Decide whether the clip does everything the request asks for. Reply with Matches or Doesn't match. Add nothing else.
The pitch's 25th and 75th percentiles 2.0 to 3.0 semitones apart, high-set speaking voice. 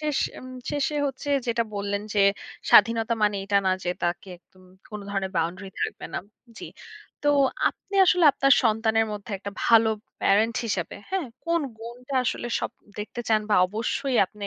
Doesn't match